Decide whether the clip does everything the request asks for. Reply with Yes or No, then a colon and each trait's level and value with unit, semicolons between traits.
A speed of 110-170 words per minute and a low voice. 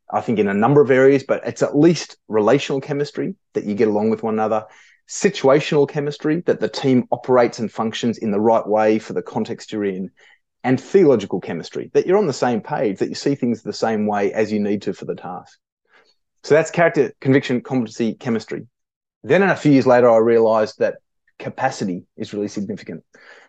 No: average, 200 wpm; low, 120 Hz